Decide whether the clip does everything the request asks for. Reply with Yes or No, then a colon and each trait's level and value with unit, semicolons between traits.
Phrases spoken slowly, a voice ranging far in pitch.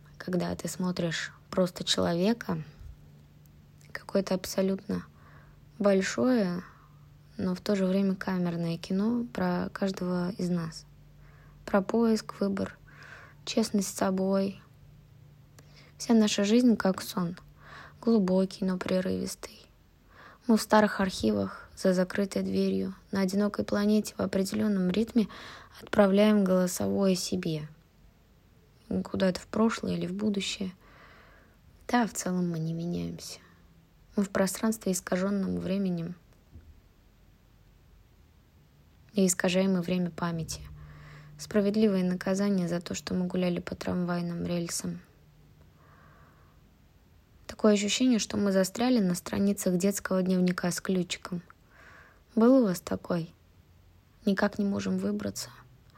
Yes: slow, 105 wpm; wide, 5.9 semitones